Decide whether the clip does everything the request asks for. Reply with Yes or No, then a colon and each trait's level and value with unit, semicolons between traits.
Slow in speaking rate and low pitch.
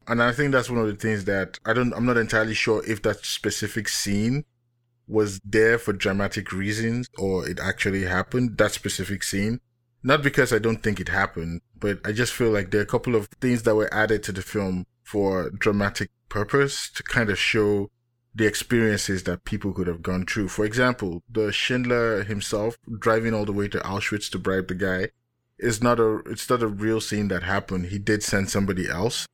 No: fast, 205 wpm; low, 105 Hz